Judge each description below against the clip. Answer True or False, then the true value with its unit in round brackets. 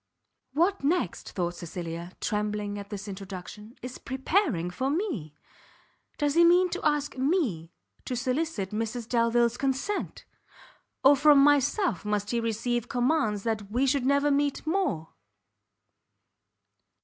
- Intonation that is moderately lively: False (5.9 semitones)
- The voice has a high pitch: True (245 Hz)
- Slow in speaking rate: True (125 wpm)